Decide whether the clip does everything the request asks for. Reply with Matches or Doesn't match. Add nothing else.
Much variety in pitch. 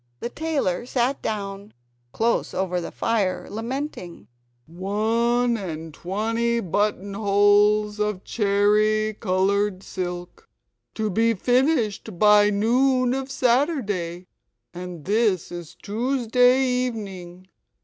Doesn't match